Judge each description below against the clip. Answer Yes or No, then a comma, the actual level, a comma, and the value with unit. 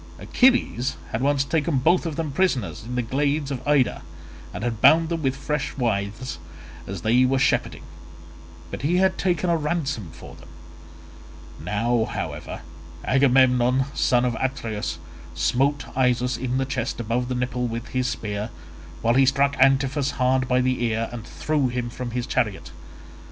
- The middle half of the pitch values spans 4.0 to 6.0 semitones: No, average, 2.8 semitones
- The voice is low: Yes, low, 130 Hz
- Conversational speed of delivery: Yes, average, 160 wpm